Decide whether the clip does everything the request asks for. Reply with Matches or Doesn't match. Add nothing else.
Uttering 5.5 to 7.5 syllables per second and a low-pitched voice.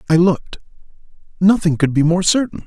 Doesn't match